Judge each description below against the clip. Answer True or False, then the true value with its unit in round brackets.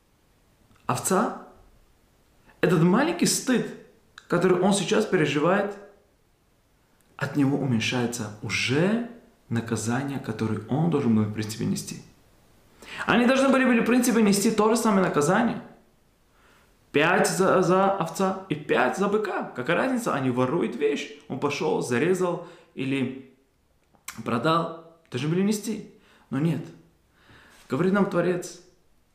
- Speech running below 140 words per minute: True (115 wpm)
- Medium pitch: True (175 Hz)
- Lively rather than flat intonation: True (7.3 semitones)